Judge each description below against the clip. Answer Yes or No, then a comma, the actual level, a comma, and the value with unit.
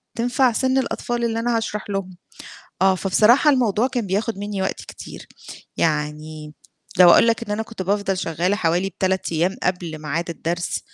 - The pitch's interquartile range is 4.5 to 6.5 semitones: Yes, average, 4.8 semitones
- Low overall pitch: No, high, 195 Hz